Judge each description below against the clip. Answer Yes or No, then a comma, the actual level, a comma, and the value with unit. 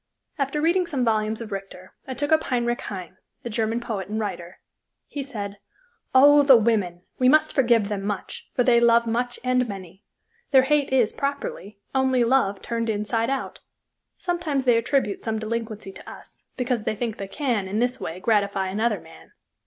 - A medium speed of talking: Yes, average, 180 wpm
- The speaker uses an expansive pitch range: No, average, 4.1 semitones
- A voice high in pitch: Yes, high, 230 Hz